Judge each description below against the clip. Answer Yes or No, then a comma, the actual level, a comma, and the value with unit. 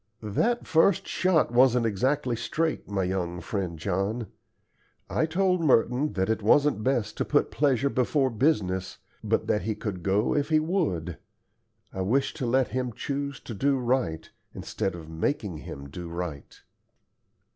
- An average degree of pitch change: No, wide, 7.0 semitones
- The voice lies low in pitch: Yes, low, 115 Hz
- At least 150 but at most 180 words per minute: Yes, average, 155 wpm